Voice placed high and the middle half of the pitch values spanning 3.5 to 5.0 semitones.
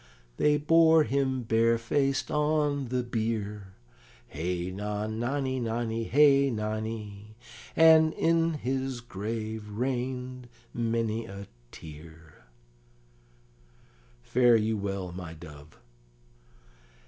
No: low, 115 Hz; average, 4.3 semitones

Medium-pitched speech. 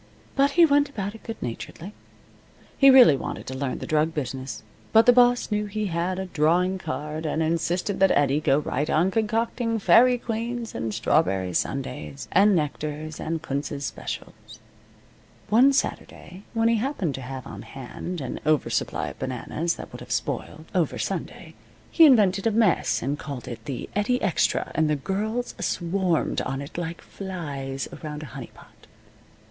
Yes: medium, 170 Hz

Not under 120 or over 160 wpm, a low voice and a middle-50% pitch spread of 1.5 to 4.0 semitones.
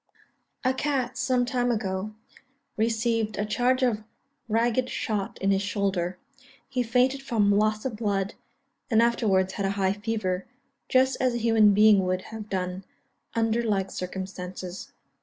No: average, 140 wpm; high, 215 Hz; average, 3.6 semitones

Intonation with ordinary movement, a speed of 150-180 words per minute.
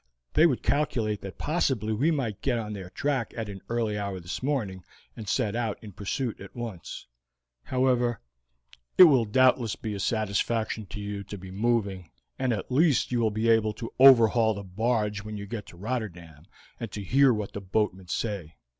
No: average, 3.4 semitones; average, 190 wpm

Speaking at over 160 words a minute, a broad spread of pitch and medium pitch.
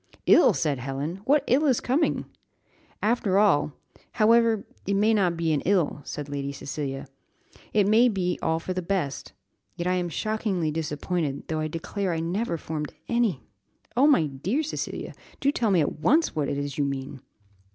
Yes: average, 180 wpm; wide, 6.5 semitones; medium, 175 Hz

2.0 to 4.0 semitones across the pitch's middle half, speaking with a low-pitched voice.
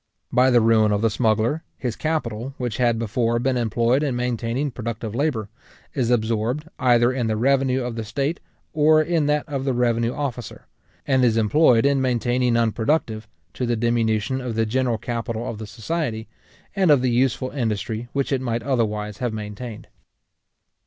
Yes: average, 2.8 semitones; low, 120 Hz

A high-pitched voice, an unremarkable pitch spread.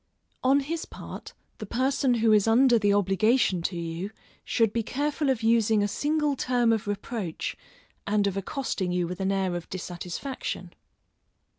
Yes: high, 220 Hz; average, 5.0 semitones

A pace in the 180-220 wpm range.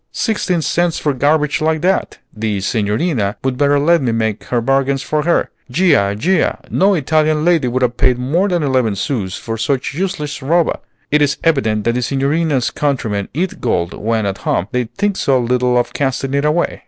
Yes: average, 190 wpm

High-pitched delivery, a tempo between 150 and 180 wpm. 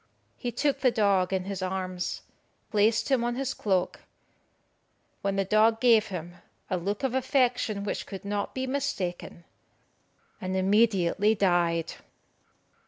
No: high, 200 Hz; slow, 135 wpm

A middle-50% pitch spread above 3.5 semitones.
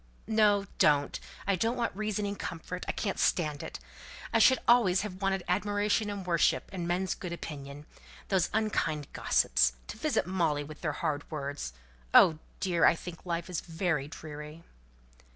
Yes: average, 4.6 semitones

